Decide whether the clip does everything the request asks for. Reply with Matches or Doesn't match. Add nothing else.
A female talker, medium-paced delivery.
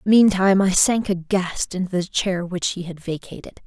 Matches